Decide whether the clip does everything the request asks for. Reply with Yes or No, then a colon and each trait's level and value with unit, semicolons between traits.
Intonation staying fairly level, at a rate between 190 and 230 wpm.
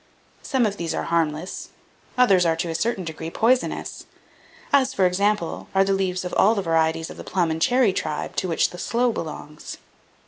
No: average, 4.5 semitones; average, 195 wpm